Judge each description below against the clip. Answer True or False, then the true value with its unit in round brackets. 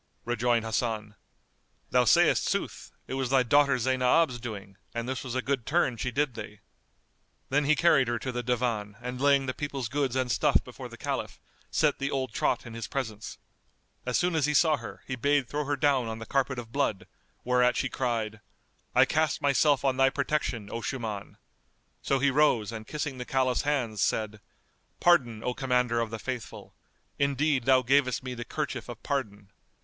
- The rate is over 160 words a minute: True (190 wpm)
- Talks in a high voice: False (130 Hz)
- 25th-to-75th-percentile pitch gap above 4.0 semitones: False (3.1 semitones)